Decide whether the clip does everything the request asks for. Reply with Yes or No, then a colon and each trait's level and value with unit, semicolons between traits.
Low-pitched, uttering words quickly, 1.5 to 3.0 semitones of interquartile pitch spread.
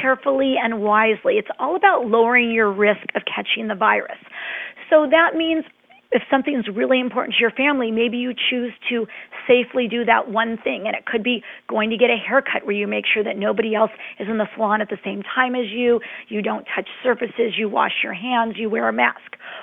No: high, 230 Hz; fast, 215 wpm; narrow, 2.6 semitones